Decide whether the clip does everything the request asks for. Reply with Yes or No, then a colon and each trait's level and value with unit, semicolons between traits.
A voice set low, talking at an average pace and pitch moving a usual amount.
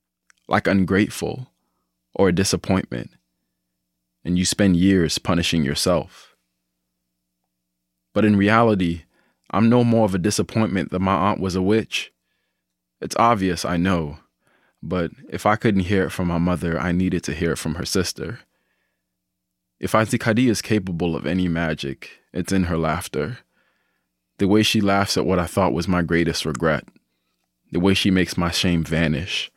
No: very low, 90 Hz; average, 155 wpm; wide, 8.1 semitones